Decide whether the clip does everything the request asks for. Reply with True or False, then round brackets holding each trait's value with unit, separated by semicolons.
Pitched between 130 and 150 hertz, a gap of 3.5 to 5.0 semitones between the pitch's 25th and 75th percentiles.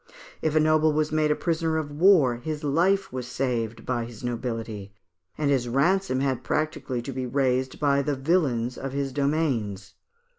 True (135 Hz; 4.0 semitones)